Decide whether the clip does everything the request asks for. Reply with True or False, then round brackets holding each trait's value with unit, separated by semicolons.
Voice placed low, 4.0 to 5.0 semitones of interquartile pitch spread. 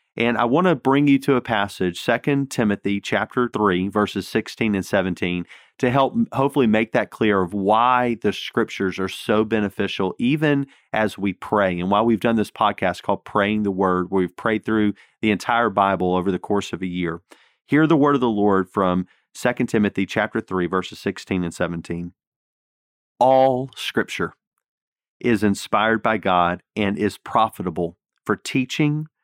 True (105 Hz; 4.3 semitones)